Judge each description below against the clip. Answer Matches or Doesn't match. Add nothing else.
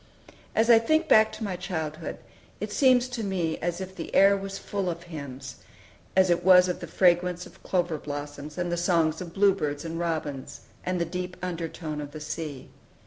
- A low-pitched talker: Doesn't match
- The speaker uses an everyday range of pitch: Matches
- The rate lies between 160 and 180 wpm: Doesn't match